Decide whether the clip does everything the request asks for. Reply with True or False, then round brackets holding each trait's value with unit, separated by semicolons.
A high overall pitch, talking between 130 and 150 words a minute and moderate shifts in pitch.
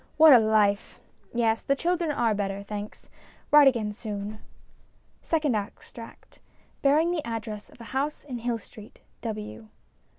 True (230 Hz; 140 wpm; 5.0 semitones)